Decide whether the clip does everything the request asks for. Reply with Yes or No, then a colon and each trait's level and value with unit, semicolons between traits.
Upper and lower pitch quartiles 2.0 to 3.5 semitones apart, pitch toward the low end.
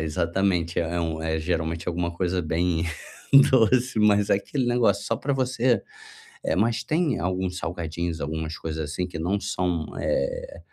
No: wide, 5.6 semitones; very low, 90 Hz